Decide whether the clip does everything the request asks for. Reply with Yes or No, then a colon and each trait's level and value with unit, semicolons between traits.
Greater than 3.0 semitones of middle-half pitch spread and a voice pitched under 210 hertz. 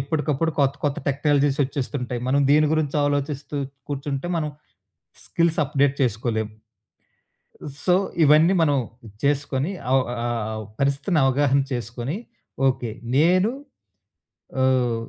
No: narrow, 2.4 semitones; medium, 140 Hz